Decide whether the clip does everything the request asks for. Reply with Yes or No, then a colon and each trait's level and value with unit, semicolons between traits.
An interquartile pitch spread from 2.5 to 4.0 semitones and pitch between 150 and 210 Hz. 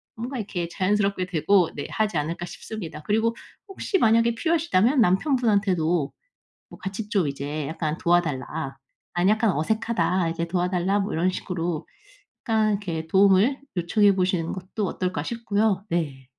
No: average, 4.4 semitones; medium, 185 Hz